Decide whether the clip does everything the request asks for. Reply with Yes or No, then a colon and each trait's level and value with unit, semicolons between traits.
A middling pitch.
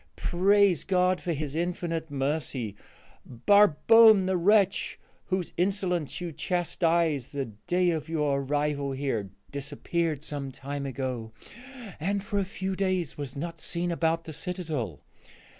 Yes: medium, 165 Hz